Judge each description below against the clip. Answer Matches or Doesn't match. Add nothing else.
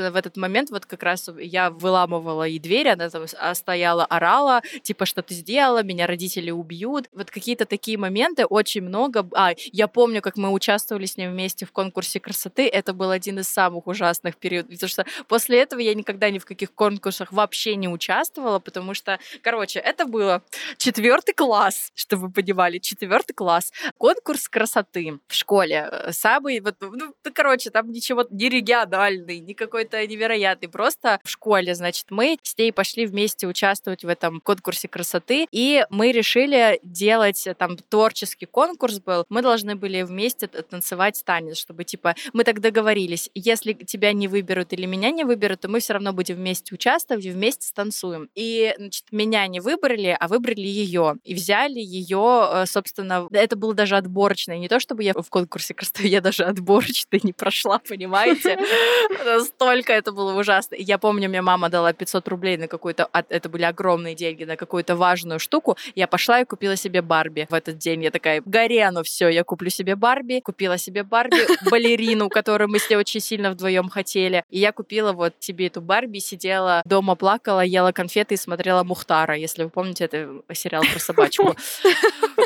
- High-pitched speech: Matches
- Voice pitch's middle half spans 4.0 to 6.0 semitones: Doesn't match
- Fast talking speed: Matches